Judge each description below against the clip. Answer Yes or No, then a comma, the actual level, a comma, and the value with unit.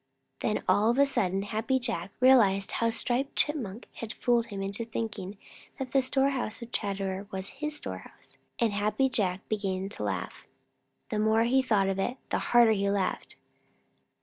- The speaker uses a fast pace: No, average, 170 wpm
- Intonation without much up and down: No, average, 4.0 semitones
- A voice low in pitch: No, high, 220 Hz